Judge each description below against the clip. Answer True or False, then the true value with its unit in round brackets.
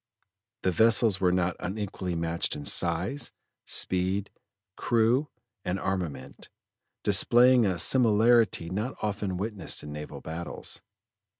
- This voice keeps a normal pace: False (110 wpm)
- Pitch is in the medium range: False (95 Hz)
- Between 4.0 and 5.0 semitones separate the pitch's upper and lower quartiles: True (4.4 semitones)